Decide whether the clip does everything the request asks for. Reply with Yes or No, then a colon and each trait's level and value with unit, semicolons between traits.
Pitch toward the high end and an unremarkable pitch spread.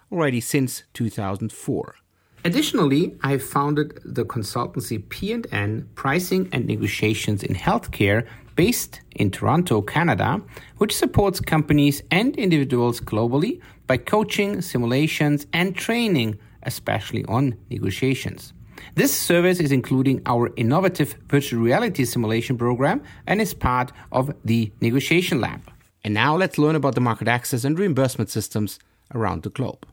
No: low, 130 Hz; average, 4.9 semitones